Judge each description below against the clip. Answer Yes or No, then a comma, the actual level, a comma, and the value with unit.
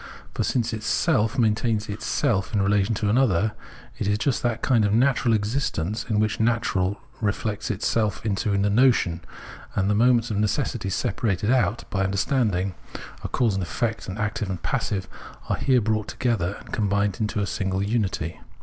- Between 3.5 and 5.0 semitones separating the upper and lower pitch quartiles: No, average, 2.7 semitones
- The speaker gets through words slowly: No, average, 185 wpm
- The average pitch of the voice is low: Yes, low, 105 Hz